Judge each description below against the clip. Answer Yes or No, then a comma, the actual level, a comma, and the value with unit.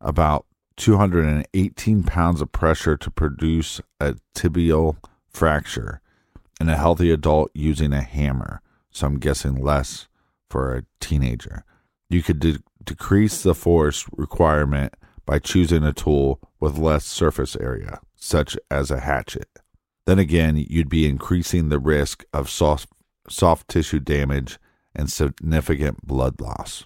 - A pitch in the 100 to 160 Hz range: No, very low, 75 Hz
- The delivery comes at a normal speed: No, slow, 130 wpm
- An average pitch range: Yes, average, 3.0 semitones